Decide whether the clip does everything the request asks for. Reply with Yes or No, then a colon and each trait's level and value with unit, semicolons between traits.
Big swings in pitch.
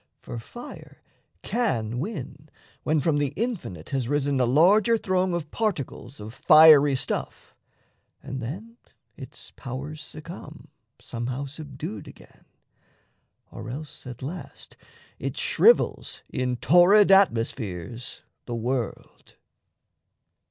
Yes: wide, 6.1 semitones